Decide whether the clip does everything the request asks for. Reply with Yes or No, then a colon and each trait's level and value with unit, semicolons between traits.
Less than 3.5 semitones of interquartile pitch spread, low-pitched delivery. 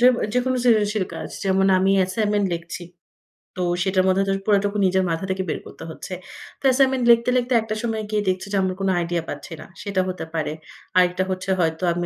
No: average, 2.8 semitones; high, 190 Hz